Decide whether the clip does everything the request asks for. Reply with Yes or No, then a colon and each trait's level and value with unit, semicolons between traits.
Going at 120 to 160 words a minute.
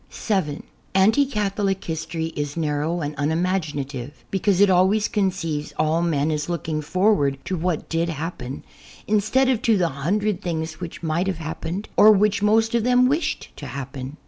No: average, 170 wpm